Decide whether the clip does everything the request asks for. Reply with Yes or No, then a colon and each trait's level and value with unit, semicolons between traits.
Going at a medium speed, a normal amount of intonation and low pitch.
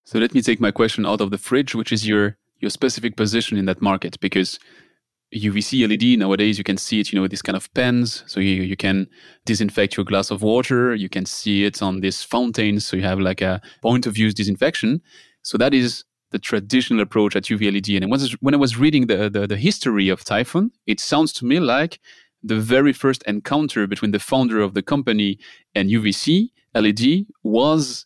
No: fast, 210 wpm; average, 3.7 semitones; low, 105 Hz